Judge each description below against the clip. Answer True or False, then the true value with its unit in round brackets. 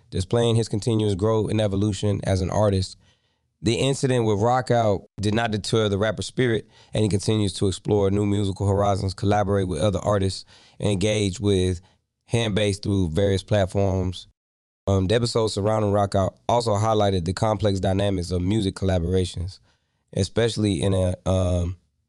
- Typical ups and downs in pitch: False (2.1 semitones)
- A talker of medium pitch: False (100 Hz)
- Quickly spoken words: False (150 wpm)